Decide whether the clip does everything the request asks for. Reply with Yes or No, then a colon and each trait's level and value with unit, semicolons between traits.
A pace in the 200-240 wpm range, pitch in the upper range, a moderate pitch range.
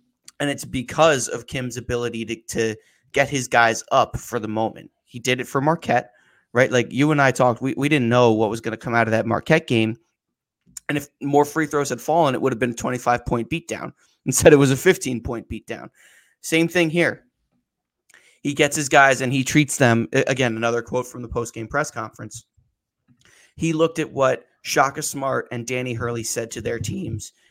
No: fast, 205 wpm; low, 125 Hz; average, 3.6 semitones